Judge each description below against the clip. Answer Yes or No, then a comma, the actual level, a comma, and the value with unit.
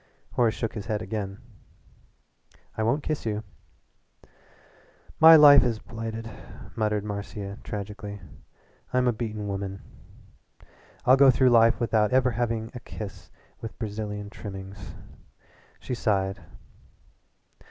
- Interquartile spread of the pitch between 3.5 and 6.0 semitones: No, average, 2.7 semitones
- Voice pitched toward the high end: No, low, 110 Hz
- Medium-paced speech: No, slow, 115 wpm